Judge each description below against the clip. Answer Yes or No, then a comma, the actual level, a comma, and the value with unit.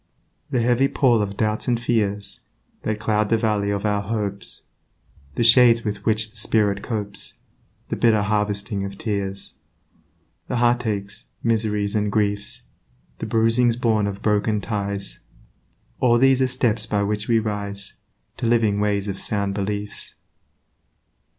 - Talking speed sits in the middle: Yes, average, 145 wpm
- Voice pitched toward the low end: Yes, low, 105 Hz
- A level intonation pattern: Yes, narrow, 2.1 semitones